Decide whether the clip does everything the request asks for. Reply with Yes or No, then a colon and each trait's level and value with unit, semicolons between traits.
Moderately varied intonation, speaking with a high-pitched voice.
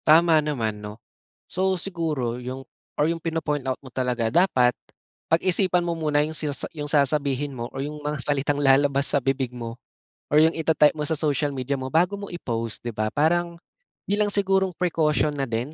No: average, 4.0 semitones; medium, 150 Hz